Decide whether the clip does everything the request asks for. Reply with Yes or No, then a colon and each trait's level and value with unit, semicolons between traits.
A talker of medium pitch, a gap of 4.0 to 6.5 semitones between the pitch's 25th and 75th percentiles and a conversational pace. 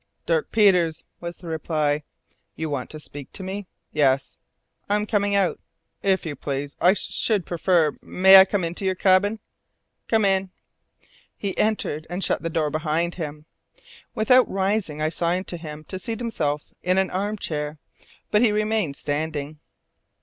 Yes: medium, 180 Hz; average, 4.6 semitones; average, 165 wpm